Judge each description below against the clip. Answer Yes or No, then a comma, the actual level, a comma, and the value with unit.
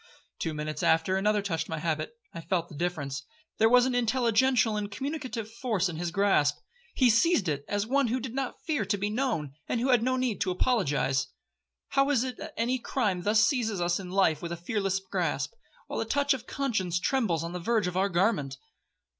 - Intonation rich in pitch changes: Yes, wide, 6.3 semitones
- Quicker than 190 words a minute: Yes, fast, 205 wpm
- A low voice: No, high, 205 Hz